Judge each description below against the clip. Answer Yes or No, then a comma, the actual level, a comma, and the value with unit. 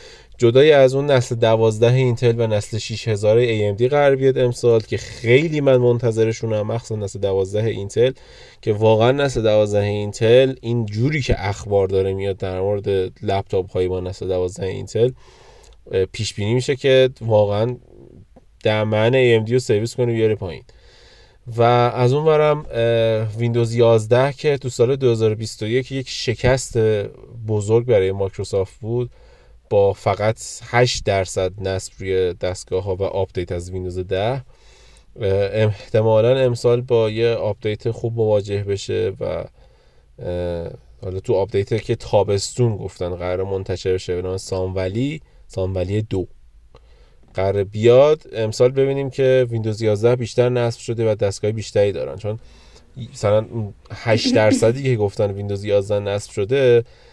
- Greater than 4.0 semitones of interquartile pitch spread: No, average, 3.4 semitones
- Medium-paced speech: Yes, average, 140 wpm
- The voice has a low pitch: Yes, low, 110 Hz